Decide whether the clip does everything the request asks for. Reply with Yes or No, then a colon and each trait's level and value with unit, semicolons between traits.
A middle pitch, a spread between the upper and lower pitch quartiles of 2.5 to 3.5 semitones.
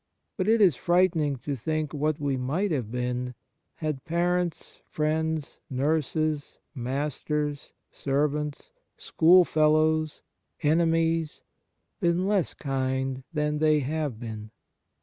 Yes: medium, 150 Hz; average, 3.0 semitones